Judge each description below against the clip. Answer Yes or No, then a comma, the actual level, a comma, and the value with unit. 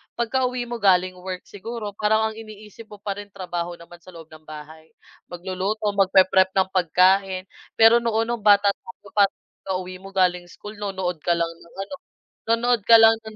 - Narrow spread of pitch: No, average, 3.1 semitones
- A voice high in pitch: Yes, high, 195 Hz